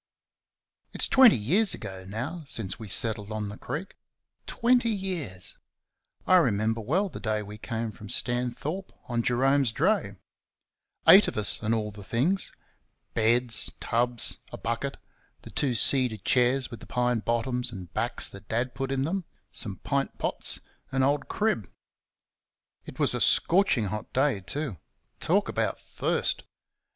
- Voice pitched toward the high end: No, low, 120 Hz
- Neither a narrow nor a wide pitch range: Yes, average, 4.9 semitones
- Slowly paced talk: No, average, 150 wpm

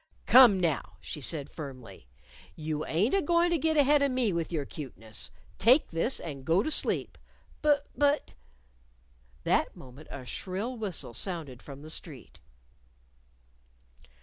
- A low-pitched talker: No, medium, 165 Hz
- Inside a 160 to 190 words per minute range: No, average, 150 wpm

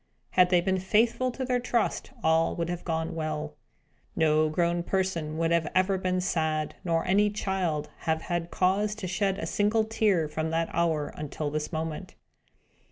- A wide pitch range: No, average, 3.3 semitones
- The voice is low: No, medium, 170 Hz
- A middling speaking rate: Yes, average, 170 wpm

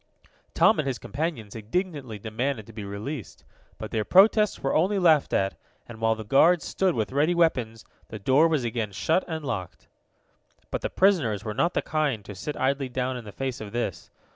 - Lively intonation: Yes, wide, 6.3 semitones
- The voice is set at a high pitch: No, low, 130 Hz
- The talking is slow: No, average, 195 wpm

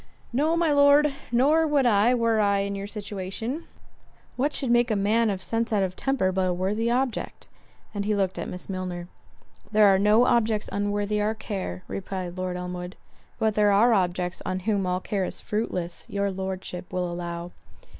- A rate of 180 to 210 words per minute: Yes, average, 185 wpm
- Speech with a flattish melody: No, average, 3.8 semitones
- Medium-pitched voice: No, high, 205 Hz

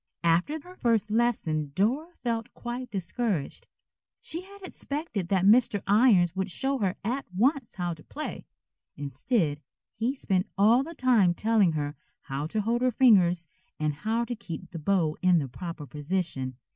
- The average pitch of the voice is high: Yes, high, 200 Hz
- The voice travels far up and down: Yes, wide, 6.3 semitones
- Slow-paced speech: No, average, 160 wpm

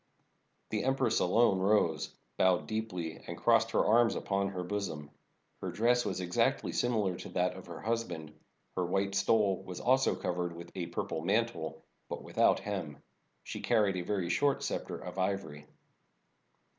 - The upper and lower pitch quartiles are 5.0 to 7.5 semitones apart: No, average, 3.9 semitones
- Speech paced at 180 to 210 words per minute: No, average, 165 wpm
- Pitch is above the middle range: No, very low, 95 Hz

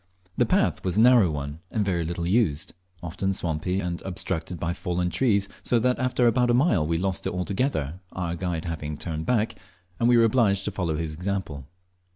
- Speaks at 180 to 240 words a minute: Yes, average, 195 wpm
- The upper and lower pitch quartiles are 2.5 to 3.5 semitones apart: No, average, 4.8 semitones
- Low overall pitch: Yes, very low, 90 Hz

